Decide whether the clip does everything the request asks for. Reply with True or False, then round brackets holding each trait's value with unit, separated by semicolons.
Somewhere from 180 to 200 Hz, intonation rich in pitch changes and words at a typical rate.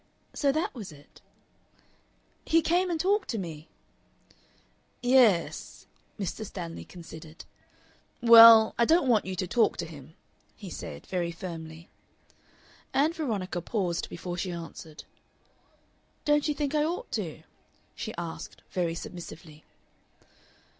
False (190 Hz; 8.2 semitones; 130 wpm)